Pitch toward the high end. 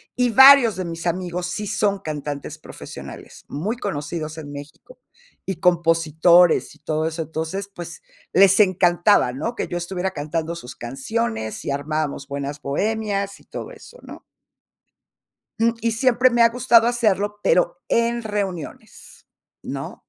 No: medium, 180 Hz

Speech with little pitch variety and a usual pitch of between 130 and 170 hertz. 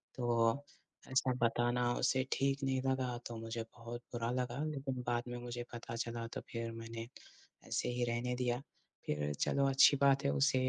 No: narrow, 2.2 semitones; low, 120 Hz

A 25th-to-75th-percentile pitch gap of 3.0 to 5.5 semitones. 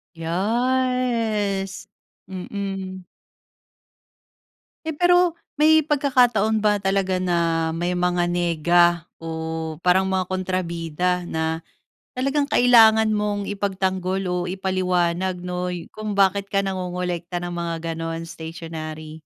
Yes: average, 3.3 semitones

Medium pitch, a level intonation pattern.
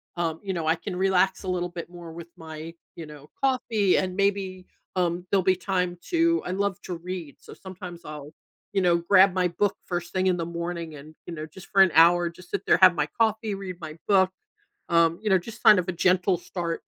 Yes: medium, 180 Hz; narrow, 2.2 semitones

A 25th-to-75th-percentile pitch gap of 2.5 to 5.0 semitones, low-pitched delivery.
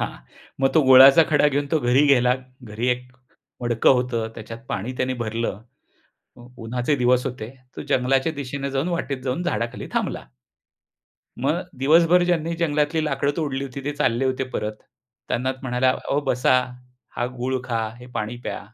Yes: average, 2.9 semitones; low, 130 Hz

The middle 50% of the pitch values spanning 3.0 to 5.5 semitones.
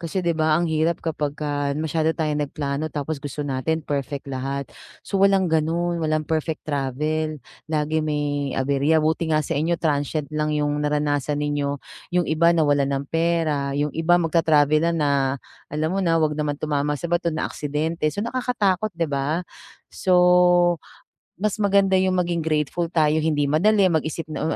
No: narrow, 2.6 semitones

